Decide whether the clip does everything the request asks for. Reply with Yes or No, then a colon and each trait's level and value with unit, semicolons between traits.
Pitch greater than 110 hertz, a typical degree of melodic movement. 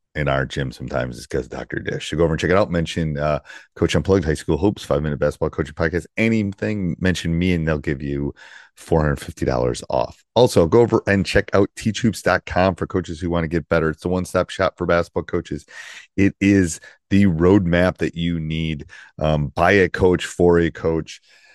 No: very low, 85 Hz; average, 3.1 semitones